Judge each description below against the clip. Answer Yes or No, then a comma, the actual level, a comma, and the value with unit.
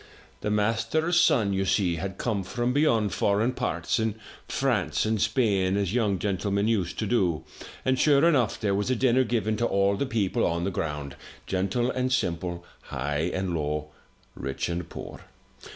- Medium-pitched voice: No, low, 100 Hz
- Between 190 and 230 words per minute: No, average, 170 wpm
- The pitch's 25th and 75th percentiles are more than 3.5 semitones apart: Yes, average, 4.9 semitones